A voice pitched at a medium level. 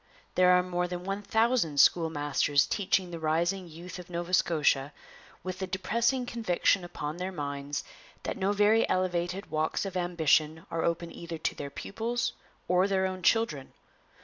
Yes: medium, 180 Hz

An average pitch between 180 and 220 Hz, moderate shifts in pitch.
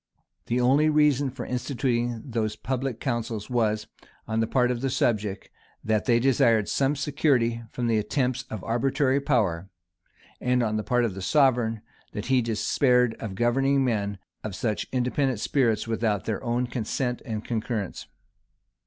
No: low, 120 Hz; average, 3.1 semitones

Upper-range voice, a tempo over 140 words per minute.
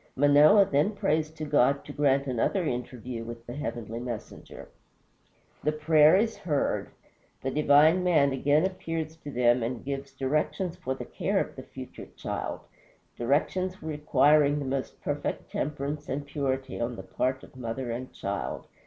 No: medium, 140 Hz; average, 160 wpm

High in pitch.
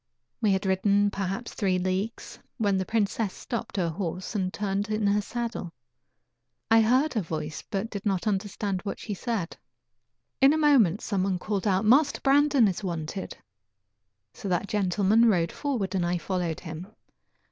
Yes: high, 200 Hz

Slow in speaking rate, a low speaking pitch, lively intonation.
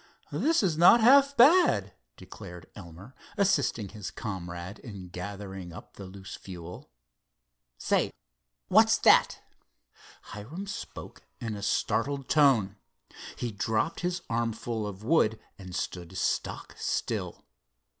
Yes: slow, 115 wpm; low, 110 Hz; wide, 7.9 semitones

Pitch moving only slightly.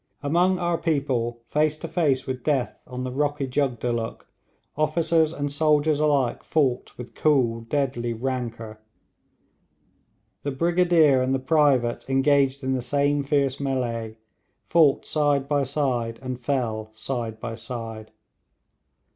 No: average, 3.5 semitones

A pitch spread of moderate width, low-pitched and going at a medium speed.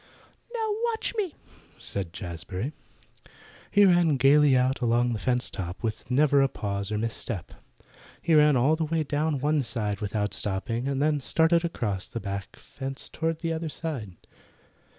No: wide, 6.6 semitones; low, 130 Hz; average, 165 wpm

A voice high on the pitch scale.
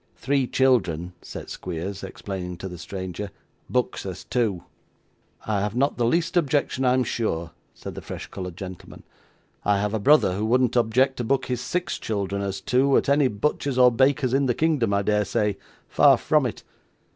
No: low, 110 Hz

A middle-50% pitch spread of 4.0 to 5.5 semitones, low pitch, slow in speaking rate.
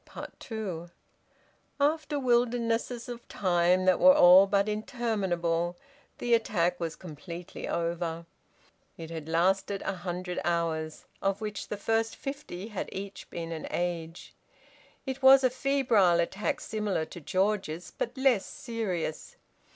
No: average, 5.1 semitones; high, 195 Hz; slow, 130 wpm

